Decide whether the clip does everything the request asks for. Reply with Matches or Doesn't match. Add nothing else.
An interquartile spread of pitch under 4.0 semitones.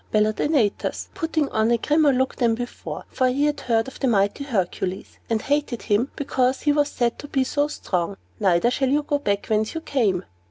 Doesn't match